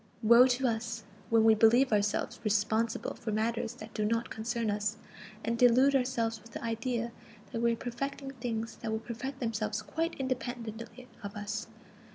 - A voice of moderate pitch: No, high, 230 Hz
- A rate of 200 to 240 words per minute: No, average, 170 wpm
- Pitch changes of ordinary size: No, narrow, 1.9 semitones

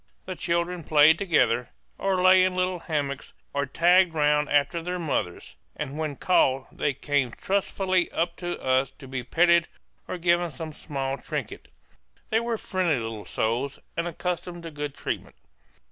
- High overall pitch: No, medium, 160 Hz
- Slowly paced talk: No, average, 160 wpm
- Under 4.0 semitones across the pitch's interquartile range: No, average, 4.3 semitones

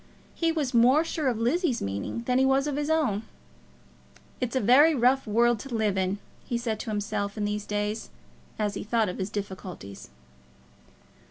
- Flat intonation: No, average, 4.4 semitones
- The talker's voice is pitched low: No, high, 230 Hz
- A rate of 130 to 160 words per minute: No, average, 180 wpm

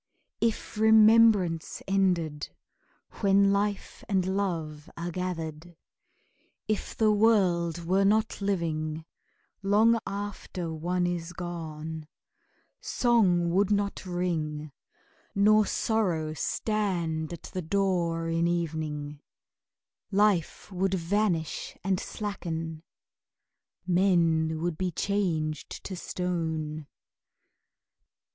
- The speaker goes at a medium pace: No, slow, 90 wpm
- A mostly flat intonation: No, average, 3.7 semitones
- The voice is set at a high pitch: No, medium, 175 Hz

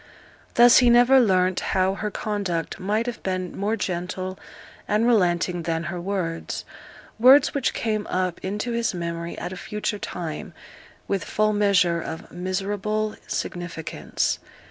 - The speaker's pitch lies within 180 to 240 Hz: Yes, high, 190 Hz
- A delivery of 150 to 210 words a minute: No, average, 140 wpm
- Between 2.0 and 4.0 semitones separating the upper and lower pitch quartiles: Yes, average, 3.3 semitones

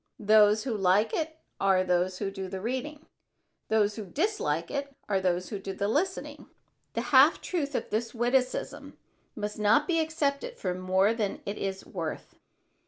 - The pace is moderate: Yes, average, 170 wpm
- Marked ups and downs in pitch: Yes, wide, 6.5 semitones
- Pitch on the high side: Yes, high, 210 Hz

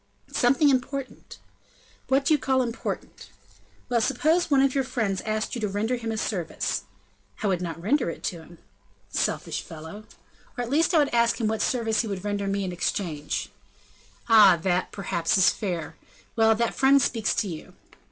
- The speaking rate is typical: Yes, average, 180 wpm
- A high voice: Yes, high, 220 Hz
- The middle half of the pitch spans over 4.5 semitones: Yes, average, 5.1 semitones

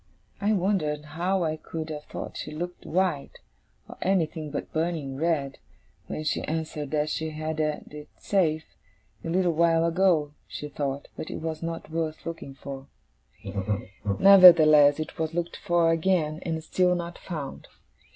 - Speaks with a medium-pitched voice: Yes, medium, 160 Hz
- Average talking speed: Yes, average, 155 wpm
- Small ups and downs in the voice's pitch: Yes, narrow, 2.2 semitones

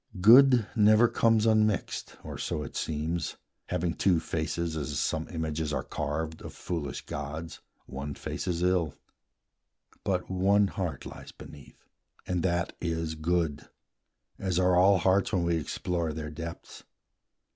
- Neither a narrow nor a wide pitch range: Yes, average, 3.0 semitones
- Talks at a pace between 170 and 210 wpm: No, average, 140 wpm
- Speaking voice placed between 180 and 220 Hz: No, very low, 85 Hz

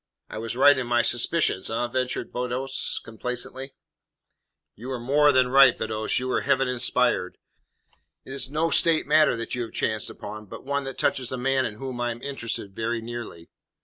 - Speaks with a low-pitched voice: Yes, low, 125 Hz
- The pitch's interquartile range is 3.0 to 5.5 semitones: No, narrow, 2.5 semitones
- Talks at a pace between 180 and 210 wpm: Yes, average, 185 wpm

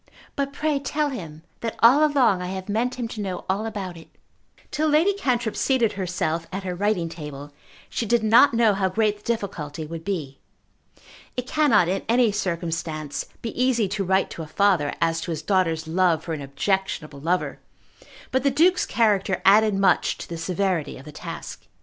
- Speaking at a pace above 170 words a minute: Yes, average, 185 wpm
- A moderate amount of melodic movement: No, wide, 5.9 semitones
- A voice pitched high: Yes, high, 195 Hz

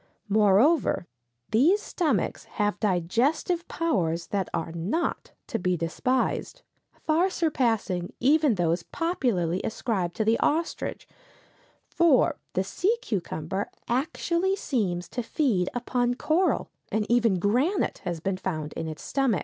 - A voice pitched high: Yes, high, 225 Hz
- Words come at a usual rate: No, slow, 125 wpm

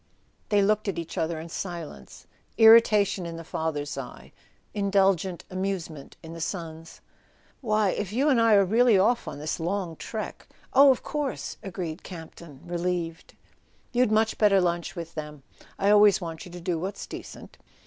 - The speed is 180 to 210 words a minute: No, average, 170 wpm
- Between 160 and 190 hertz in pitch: Yes, medium, 185 Hz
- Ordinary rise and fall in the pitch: Yes, average, 4.1 semitones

